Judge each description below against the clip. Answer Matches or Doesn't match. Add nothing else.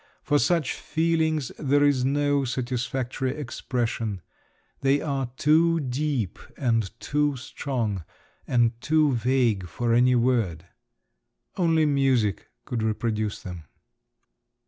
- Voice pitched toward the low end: Matches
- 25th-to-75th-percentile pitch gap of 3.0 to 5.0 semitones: Matches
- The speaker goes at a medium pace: Doesn't match